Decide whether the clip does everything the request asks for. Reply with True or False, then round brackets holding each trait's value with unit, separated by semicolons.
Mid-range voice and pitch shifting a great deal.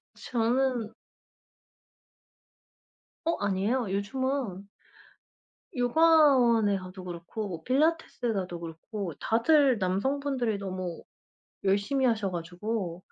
False (220 Hz; 5.7 semitones)